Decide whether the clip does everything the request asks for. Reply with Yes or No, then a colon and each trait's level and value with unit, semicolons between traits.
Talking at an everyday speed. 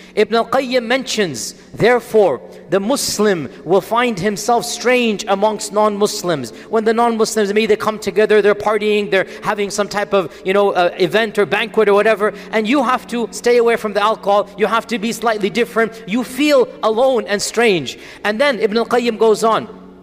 Yes: average, 180 wpm